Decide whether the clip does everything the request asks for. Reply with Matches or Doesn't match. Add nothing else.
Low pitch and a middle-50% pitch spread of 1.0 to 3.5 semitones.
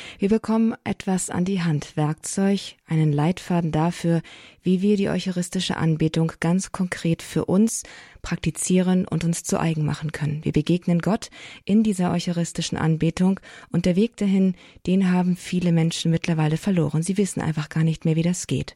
Doesn't match